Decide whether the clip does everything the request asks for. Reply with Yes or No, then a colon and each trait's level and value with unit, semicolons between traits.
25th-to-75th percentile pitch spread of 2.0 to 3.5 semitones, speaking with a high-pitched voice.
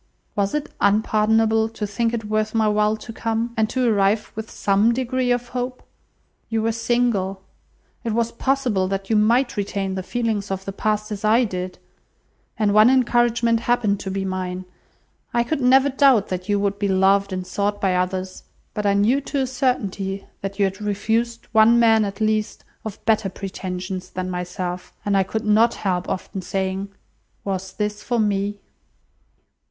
Yes: average, 2.9 semitones; high, 210 Hz